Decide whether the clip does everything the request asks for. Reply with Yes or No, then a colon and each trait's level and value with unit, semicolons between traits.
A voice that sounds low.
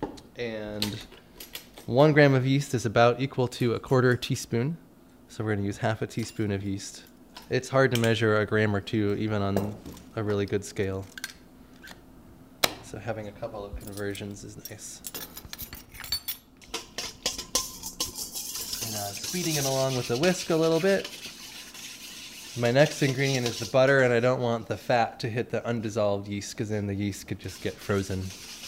Yes: low, 115 Hz